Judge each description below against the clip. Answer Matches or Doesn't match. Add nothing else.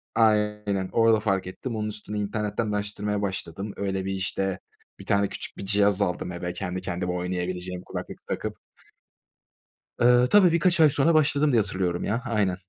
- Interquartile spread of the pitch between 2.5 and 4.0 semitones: Matches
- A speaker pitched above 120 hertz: Doesn't match